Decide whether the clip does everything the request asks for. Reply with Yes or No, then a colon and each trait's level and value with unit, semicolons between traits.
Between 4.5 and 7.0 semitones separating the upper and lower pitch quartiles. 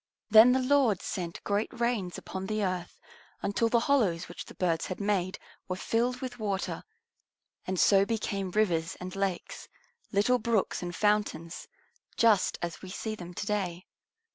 No: average, 3.4 semitones